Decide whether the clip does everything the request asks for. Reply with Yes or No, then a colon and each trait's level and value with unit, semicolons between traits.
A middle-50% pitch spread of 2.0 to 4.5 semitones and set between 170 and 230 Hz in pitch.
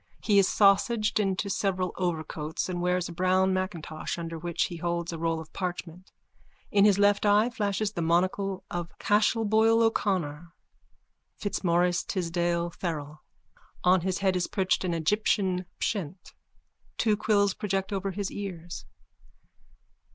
Yes: average, 2.8 semitones; medium, 185 Hz